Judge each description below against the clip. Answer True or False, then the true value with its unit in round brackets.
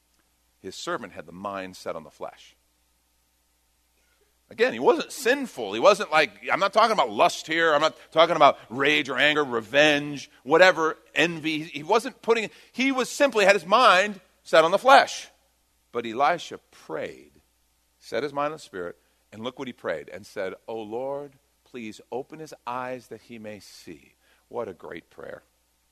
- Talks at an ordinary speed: True (175 wpm)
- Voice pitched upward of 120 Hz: True (140 Hz)